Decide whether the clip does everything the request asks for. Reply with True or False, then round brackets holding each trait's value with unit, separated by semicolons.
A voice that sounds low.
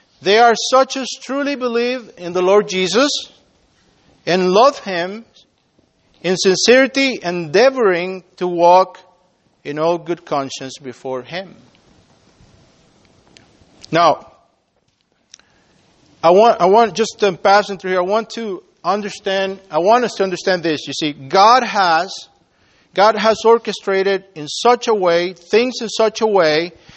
False (195 Hz)